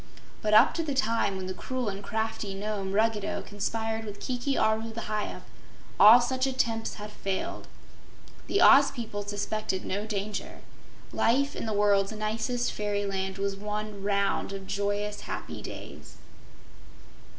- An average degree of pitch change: No, narrow, 2.1 semitones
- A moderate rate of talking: Yes, average, 145 wpm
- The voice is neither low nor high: No, high, 210 Hz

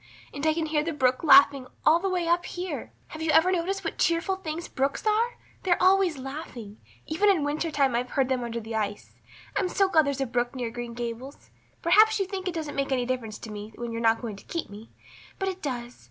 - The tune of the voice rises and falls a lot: Yes, wide, 6.4 semitones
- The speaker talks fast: Yes, fast, 235 wpm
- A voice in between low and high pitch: No, very high, 290 Hz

